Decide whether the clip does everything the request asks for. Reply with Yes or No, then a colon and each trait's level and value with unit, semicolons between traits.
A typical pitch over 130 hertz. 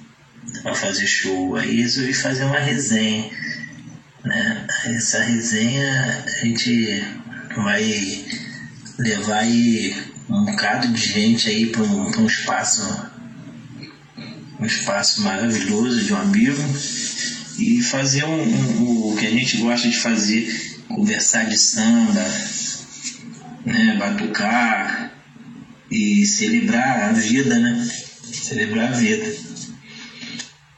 Yes: medium, 140 Hz